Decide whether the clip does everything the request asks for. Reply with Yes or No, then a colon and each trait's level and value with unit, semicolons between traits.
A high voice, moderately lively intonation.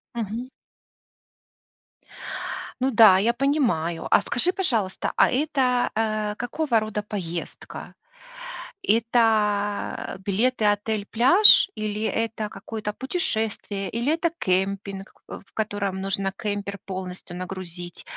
Yes: high, 215 Hz; average, 3.3 semitones